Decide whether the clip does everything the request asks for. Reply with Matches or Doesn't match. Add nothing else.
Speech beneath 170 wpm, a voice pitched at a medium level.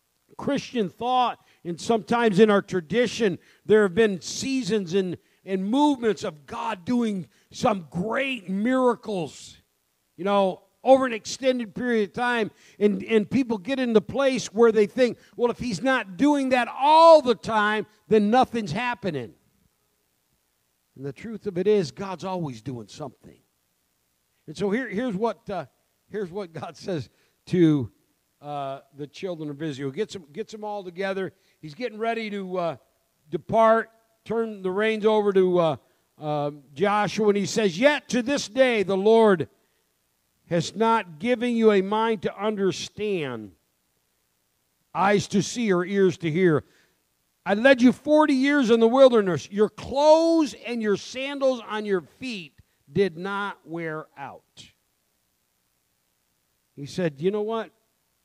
Doesn't match